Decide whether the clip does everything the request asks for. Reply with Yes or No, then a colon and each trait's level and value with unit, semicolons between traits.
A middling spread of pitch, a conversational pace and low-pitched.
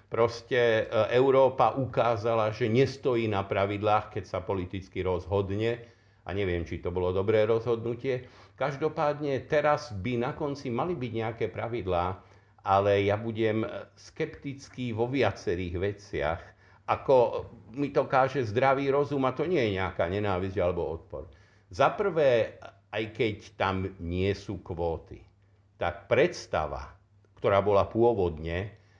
Yes: average, 4.2 semitones; average, 125 wpm; low, 110 Hz